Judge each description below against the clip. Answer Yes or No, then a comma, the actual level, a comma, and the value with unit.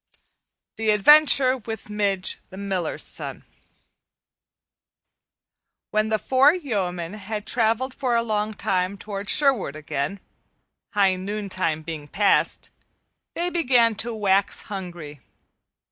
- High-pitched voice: Yes, high, 210 Hz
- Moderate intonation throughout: Yes, average, 3.8 semitones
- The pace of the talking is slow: Yes, slow, 110 wpm